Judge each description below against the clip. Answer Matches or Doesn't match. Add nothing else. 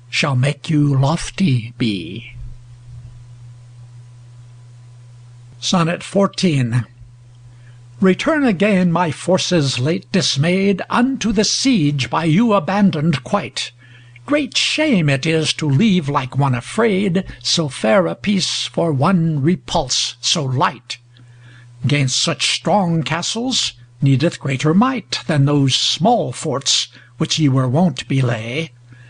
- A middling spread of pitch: Doesn't match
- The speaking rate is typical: Doesn't match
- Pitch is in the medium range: Matches